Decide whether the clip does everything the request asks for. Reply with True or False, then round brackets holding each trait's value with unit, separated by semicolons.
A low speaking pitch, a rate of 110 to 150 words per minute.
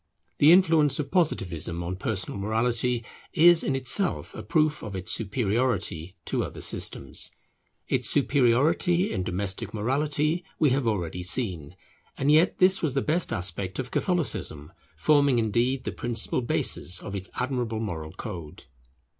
True (120 Hz; 145 wpm)